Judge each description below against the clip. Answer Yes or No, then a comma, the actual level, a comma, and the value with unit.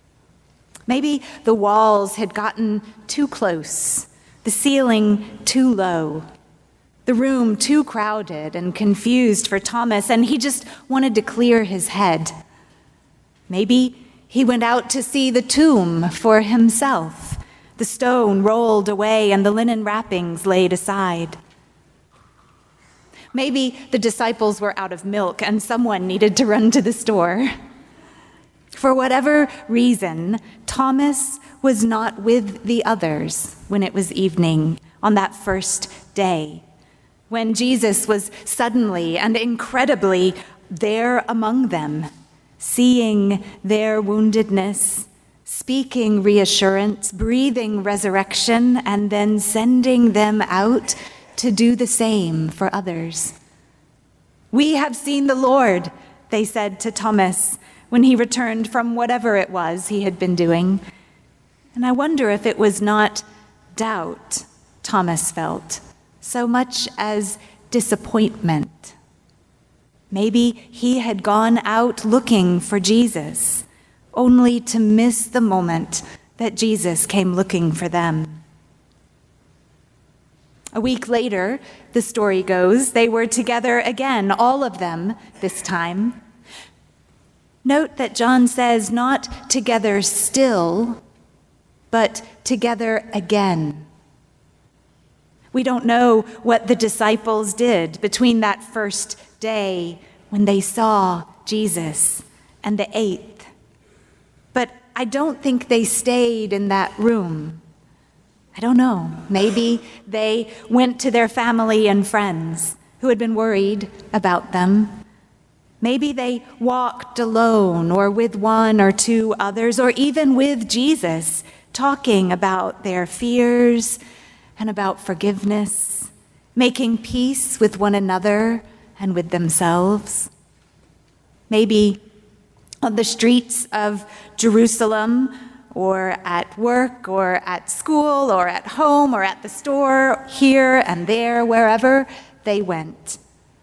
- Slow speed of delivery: Yes, slow, 120 wpm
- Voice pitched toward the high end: Yes, high, 220 Hz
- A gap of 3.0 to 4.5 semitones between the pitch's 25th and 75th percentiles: Yes, average, 3.7 semitones